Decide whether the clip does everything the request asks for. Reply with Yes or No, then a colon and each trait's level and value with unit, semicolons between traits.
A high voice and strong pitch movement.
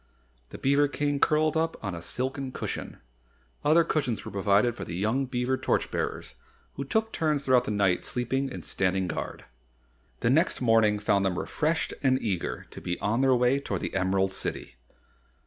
No: low, 125 Hz; wide, 5.8 semitones